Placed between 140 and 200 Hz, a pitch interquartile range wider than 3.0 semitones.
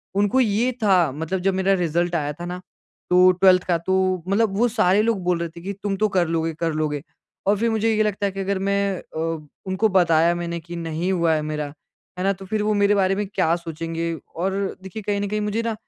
Yes: medium, 185 Hz; average, 3.4 semitones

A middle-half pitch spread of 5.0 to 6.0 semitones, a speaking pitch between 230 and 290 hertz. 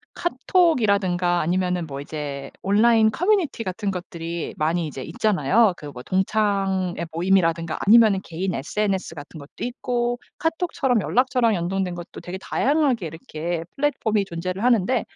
No: wide, 5.5 semitones; high, 190 Hz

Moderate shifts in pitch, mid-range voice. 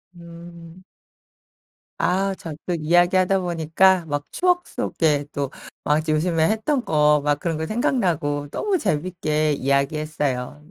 Yes: average, 3.7 semitones; medium, 165 Hz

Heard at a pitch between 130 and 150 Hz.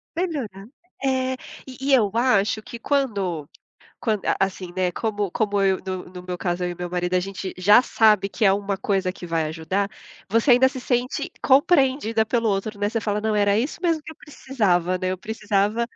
No: high, 205 Hz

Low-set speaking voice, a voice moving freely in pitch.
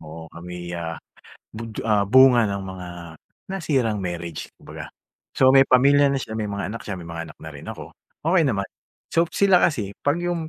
Yes: low, 105 Hz; wide, 7.5 semitones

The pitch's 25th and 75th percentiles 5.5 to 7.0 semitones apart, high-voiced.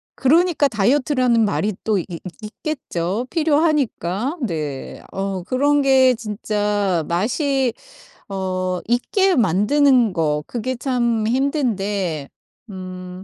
Yes: wide, 6.4 semitones; high, 220 Hz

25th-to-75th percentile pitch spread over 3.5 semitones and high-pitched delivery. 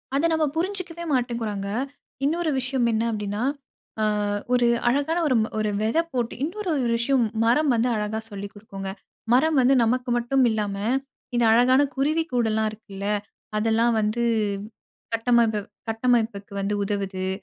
Yes: average, 3.9 semitones; high, 235 Hz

